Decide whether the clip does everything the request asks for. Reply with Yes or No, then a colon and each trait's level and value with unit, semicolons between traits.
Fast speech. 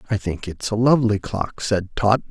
Yes: fast, 210 wpm